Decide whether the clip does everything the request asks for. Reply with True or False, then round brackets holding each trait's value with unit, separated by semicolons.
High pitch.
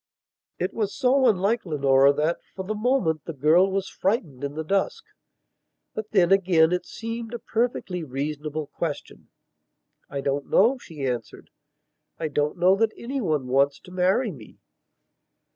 False (175 Hz)